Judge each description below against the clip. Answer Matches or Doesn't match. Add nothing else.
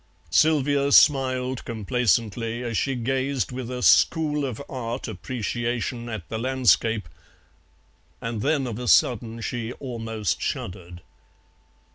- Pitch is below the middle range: Matches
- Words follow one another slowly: Matches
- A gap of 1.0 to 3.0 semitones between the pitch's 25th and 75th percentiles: Matches